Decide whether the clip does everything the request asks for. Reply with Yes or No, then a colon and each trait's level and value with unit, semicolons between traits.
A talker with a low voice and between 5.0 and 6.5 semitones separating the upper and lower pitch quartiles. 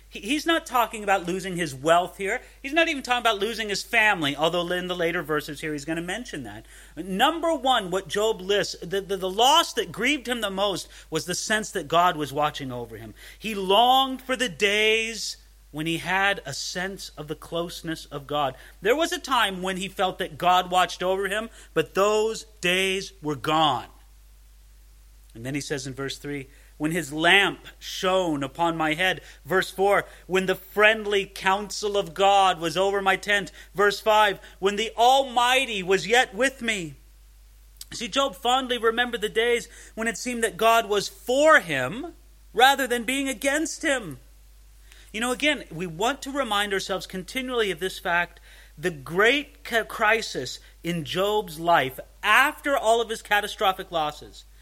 No: high, 195 Hz; average, 5.3 semitones